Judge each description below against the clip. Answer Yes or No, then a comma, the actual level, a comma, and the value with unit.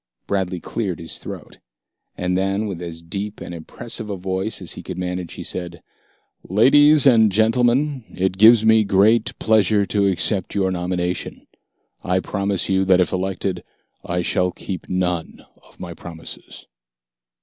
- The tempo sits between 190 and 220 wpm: No, average, 150 wpm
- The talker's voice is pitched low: Yes, very low, 95 Hz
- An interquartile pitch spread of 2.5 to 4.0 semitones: Yes, average, 3.0 semitones